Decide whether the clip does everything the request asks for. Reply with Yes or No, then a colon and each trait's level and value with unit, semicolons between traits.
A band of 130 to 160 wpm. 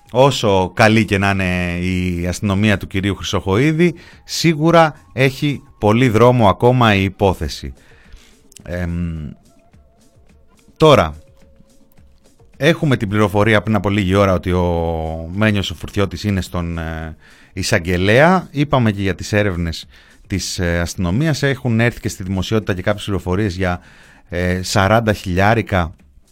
No: average, 120 wpm